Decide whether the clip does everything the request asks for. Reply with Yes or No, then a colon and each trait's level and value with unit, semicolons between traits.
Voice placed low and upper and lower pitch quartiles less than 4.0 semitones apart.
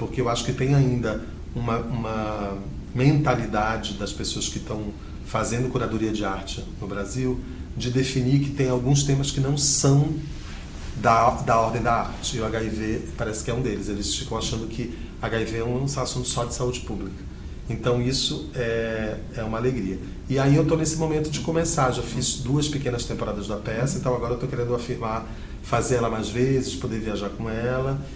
Yes: low, 120 Hz; average, 3.1 semitones